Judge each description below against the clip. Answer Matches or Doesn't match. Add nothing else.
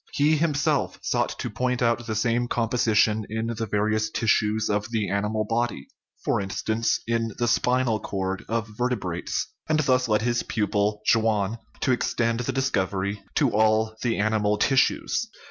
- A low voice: Matches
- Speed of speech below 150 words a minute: Doesn't match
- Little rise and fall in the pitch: Matches